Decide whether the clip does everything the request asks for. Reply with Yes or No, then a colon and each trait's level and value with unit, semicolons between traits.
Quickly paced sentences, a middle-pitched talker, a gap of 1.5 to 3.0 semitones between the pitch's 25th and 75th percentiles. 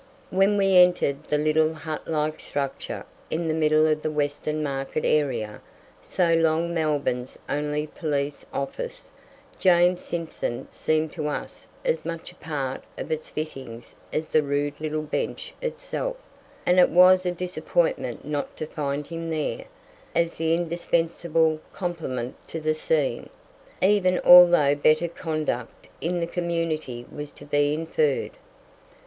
No: average, 140 wpm; medium, 155 Hz; narrow, 2.6 semitones